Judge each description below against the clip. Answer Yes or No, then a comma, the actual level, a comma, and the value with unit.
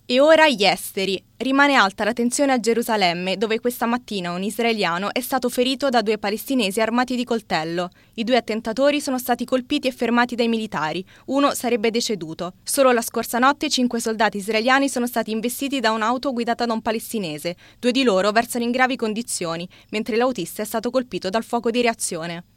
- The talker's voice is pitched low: No, high, 235 Hz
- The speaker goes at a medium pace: No, fast, 185 wpm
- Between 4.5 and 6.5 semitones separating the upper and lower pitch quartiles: No, average, 3.0 semitones